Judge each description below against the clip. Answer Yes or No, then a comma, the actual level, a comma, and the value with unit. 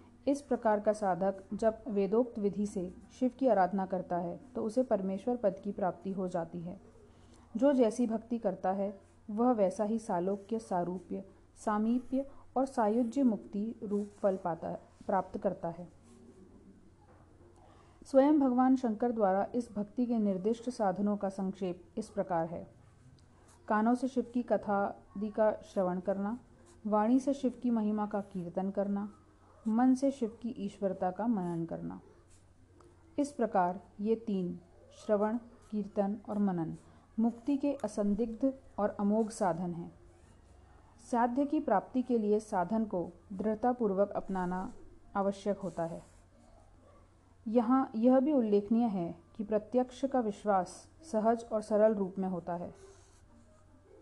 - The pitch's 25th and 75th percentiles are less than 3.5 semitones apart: No, average, 4.2 semitones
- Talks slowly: No, average, 135 wpm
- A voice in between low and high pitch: No, high, 205 Hz